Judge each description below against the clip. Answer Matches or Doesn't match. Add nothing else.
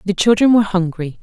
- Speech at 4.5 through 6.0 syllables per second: Doesn't match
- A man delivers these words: Doesn't match